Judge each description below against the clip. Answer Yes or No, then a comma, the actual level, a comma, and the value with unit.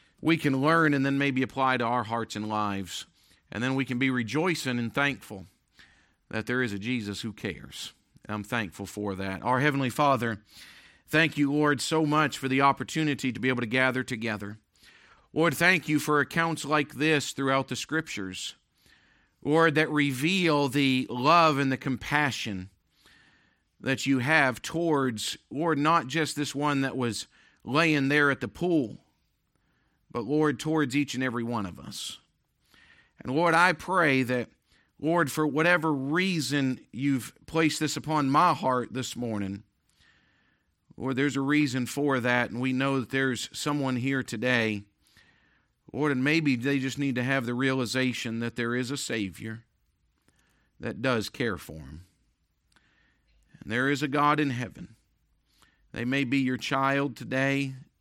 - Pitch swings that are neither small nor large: Yes, average, 4.0 semitones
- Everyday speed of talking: Yes, average, 160 wpm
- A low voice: Yes, low, 130 Hz